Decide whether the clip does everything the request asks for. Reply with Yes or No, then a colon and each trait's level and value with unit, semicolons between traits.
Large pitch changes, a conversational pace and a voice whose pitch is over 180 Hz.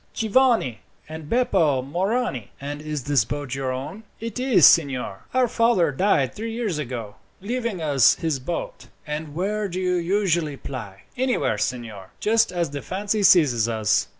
No: wide, 7.8 semitones; average, 155 wpm; medium, 160 Hz